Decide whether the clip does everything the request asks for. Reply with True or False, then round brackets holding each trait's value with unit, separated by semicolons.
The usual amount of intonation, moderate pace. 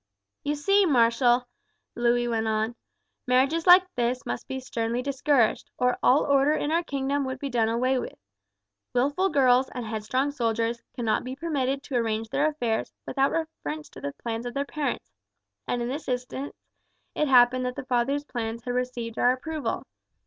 True (3.0 semitones; 170 wpm)